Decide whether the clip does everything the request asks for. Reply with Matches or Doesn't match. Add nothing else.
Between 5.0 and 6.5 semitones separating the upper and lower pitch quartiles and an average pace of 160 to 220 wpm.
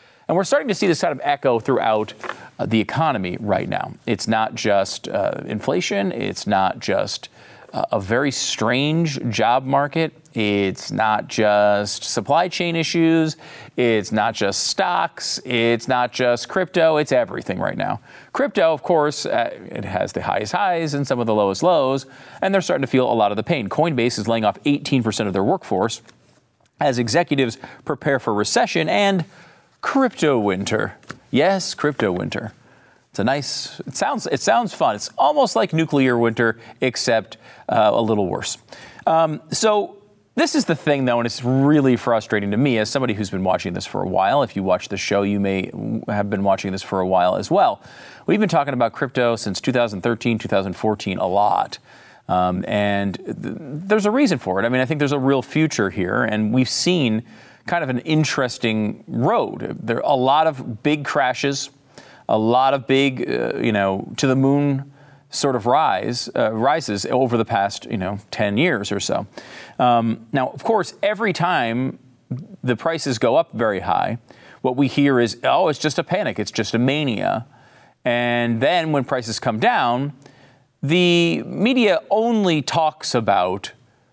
Matches